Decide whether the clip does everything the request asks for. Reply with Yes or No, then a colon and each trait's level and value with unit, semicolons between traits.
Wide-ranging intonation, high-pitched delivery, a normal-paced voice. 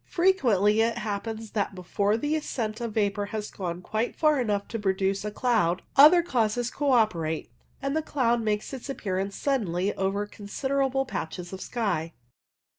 No: average, 4.3 semitones; high, 215 Hz; average, 160 wpm